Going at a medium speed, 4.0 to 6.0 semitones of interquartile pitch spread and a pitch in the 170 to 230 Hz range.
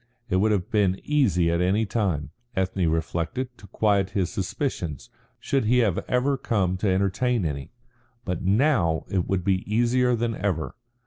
No: average, 165 wpm; average, 4.6 semitones; low, 100 Hz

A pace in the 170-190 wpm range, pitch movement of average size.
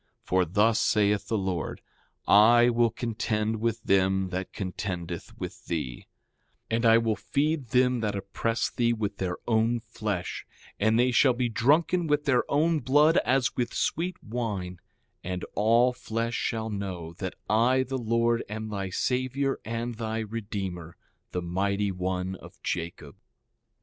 No: average, 150 wpm; average, 3.9 semitones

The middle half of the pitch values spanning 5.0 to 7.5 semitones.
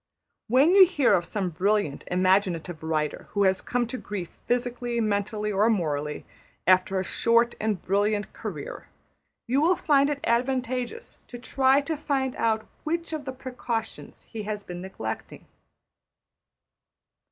Yes: wide, 5.4 semitones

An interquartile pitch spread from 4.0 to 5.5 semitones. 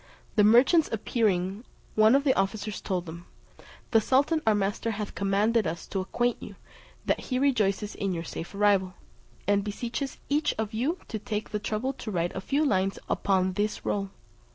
No: average, 3.5 semitones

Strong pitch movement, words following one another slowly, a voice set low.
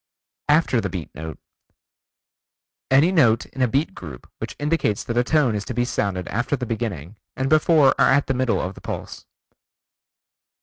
No: wide, 5.7 semitones; average, 175 wpm; low, 120 Hz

